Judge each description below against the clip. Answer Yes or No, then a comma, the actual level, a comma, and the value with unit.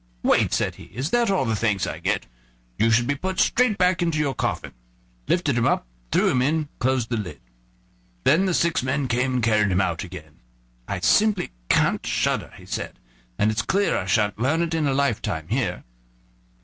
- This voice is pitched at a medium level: No, low, 130 Hz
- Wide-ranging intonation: Yes, wide, 7.2 semitones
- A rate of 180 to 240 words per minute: Yes, average, 200 wpm